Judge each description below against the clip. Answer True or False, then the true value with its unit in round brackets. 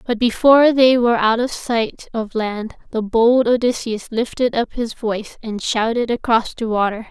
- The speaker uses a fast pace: False (175 wpm)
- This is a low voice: False (230 Hz)